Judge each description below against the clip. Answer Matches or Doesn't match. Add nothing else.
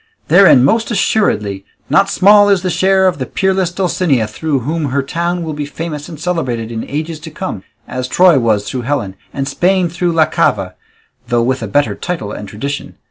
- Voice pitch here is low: Doesn't match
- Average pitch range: Doesn't match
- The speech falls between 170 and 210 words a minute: Matches